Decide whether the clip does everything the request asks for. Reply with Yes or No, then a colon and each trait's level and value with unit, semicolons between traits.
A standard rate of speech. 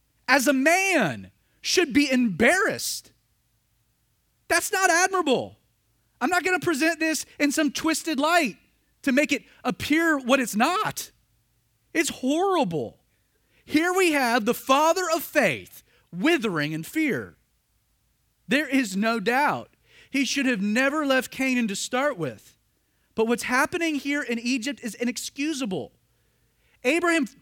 No: slow, 130 wpm